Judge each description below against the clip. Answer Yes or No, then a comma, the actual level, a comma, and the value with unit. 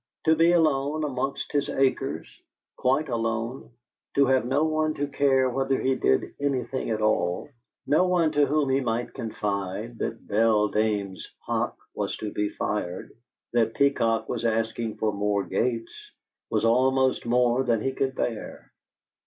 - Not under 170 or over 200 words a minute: No, average, 150 wpm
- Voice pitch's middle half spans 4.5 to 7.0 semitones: No, average, 3.8 semitones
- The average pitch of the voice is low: Yes, low, 125 Hz